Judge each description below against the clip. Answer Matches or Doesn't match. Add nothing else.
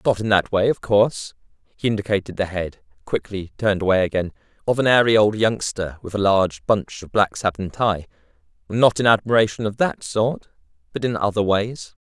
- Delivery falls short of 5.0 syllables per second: Doesn't match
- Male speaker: Matches